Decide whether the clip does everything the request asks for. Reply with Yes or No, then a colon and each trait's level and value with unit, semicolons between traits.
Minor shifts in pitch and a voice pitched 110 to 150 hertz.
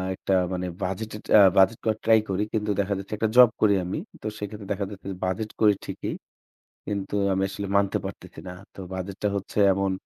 No: narrow, 1.9 semitones; low, 100 Hz